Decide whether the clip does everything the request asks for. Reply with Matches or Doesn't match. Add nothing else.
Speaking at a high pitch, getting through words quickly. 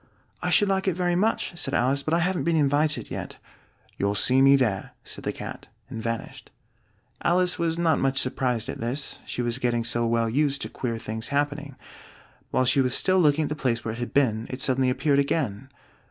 Doesn't match